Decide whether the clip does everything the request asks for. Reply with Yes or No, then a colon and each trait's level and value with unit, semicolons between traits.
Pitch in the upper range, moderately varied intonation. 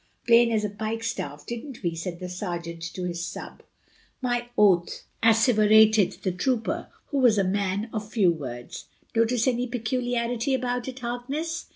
Yes: high, 220 Hz; average, 4.8 semitones